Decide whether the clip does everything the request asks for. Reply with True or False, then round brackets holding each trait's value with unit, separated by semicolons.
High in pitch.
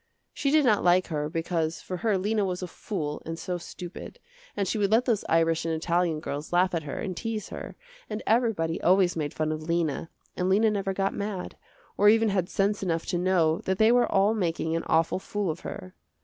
False (180 Hz)